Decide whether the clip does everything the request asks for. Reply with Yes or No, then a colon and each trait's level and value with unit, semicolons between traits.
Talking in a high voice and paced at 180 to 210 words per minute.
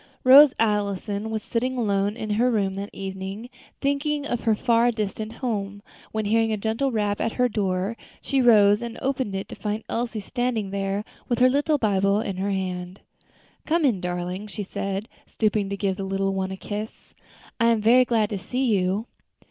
Yes: high, 215 Hz; average, 190 wpm